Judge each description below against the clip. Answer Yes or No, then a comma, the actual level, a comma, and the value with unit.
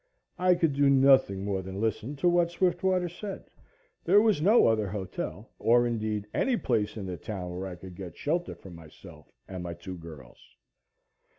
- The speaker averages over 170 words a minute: Yes, average, 180 wpm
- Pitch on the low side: Yes, low, 110 Hz